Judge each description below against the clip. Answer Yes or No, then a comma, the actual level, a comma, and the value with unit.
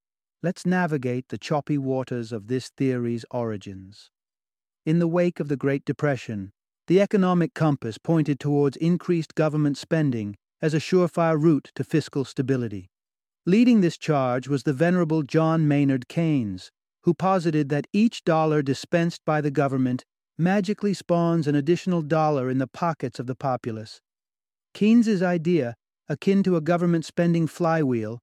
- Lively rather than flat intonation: No, average, 4.8 semitones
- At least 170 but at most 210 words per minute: No, average, 145 wpm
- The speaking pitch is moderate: Yes, medium, 150 Hz